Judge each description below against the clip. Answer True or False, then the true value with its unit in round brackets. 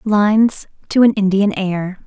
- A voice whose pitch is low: False (200 Hz)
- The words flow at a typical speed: True (145 wpm)